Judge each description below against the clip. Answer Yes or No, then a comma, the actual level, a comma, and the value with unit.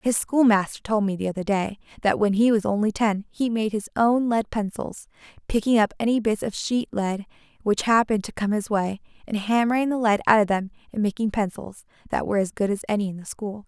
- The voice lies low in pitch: No, high, 215 Hz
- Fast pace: Yes, fast, 225 wpm